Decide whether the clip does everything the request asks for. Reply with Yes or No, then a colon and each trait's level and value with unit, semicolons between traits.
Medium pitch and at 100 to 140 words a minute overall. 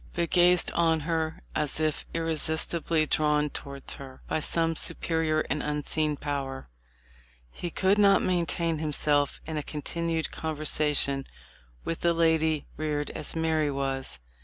Yes: medium, 155 Hz; slow, 135 wpm